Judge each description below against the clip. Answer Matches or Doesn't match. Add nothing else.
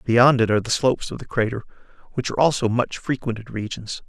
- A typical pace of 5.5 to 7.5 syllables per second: Matches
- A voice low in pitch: Matches